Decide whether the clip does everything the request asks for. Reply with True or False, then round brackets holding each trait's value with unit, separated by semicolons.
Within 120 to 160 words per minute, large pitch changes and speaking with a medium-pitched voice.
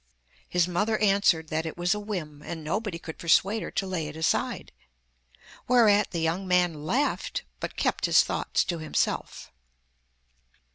False (155 wpm; 4.2 semitones; 175 Hz)